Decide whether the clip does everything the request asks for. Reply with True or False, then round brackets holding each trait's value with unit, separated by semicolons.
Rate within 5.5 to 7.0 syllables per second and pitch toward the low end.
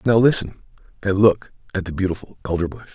True (6.5 syllables/s; 100 Hz)